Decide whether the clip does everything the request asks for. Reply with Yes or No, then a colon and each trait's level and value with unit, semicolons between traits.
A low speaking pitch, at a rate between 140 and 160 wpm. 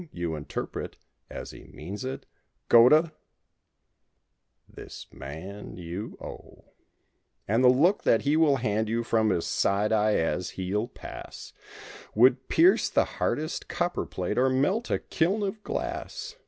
Yes: low, 115 Hz; average, 145 wpm